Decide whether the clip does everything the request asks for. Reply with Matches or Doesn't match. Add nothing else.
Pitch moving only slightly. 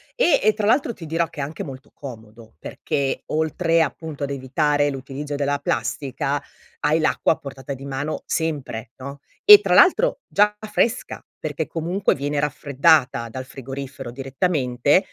Doesn't match